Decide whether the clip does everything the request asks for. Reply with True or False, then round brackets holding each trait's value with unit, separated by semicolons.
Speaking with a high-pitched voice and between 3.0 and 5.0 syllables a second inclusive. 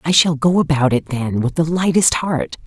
False (150 Hz; 4.8 syllables/s)